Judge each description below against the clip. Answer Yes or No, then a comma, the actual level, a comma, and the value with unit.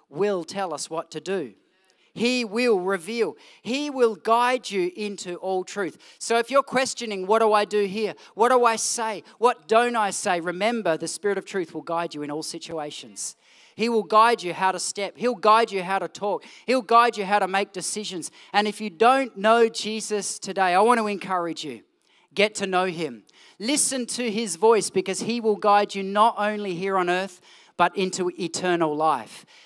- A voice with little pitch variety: No, average, 3.9 semitones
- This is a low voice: No, high, 205 Hz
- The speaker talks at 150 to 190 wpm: No, average, 200 wpm